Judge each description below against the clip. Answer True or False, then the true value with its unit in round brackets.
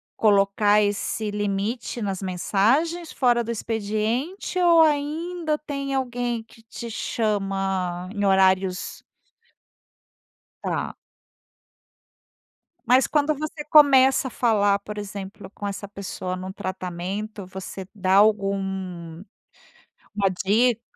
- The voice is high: True (210 Hz)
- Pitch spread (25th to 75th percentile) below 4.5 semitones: False (4.9 semitones)